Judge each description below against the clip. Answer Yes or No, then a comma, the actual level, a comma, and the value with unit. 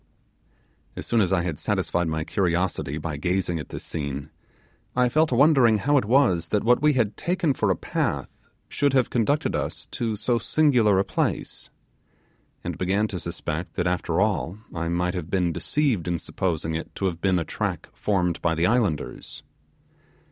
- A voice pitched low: Yes, very low, 95 Hz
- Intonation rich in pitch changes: Yes, wide, 6.0 semitones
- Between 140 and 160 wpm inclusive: No, average, 180 wpm